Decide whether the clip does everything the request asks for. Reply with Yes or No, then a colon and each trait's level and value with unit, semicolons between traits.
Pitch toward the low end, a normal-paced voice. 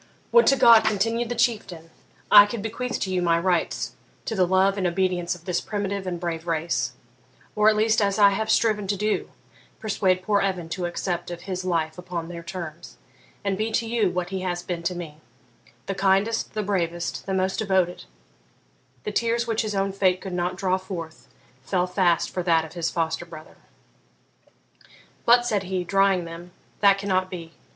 No: medium, 185 Hz; average, 190 wpm